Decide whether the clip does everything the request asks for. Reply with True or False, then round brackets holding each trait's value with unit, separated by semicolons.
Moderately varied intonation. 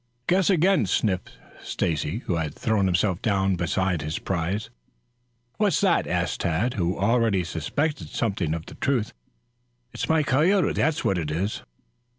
False (7.1 semitones)